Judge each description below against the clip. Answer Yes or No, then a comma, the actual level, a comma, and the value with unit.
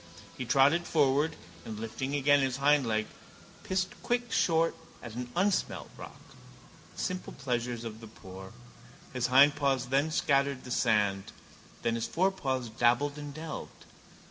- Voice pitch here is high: No, low, 135 Hz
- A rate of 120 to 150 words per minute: Yes, average, 140 wpm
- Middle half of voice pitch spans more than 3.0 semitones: Yes, average, 4.0 semitones